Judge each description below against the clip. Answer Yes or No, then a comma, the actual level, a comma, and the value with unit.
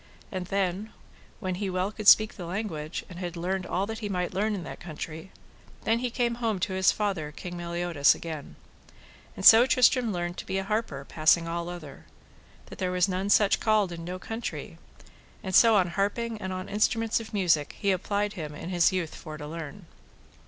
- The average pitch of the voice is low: No, medium, 185 Hz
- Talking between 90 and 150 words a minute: No, average, 200 wpm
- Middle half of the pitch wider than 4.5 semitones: No, average, 3.5 semitones